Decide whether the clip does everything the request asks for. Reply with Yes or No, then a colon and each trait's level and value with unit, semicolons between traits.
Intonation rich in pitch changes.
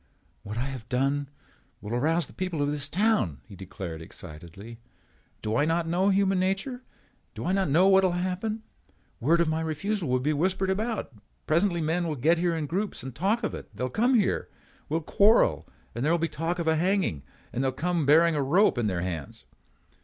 Yes: wide, 6.3 semitones